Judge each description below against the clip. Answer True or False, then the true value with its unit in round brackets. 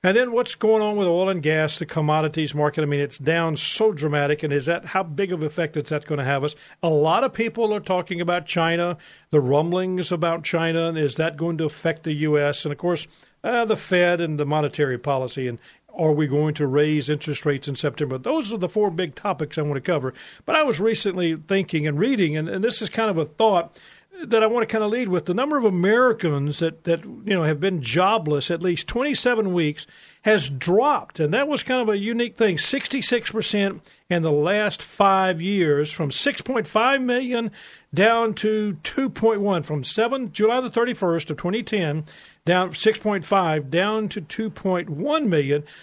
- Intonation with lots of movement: True (6.0 semitones)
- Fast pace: True (215 wpm)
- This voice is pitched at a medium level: True (175 Hz)